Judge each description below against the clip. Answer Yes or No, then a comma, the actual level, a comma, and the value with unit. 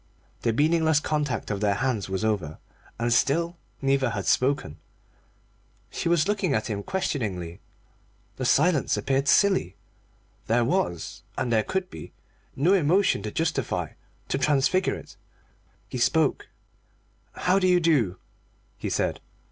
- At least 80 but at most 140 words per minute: Yes, slow, 135 wpm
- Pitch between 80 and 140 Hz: Yes, low, 135 Hz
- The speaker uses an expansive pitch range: Yes, wide, 7.7 semitones